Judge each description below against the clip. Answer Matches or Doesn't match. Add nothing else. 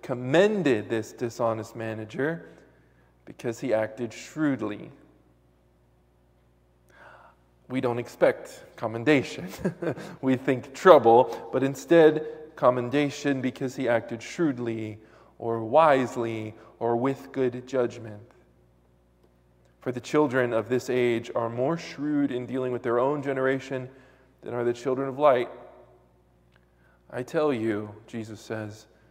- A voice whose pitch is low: Matches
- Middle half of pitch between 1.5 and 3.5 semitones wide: Doesn't match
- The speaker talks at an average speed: Doesn't match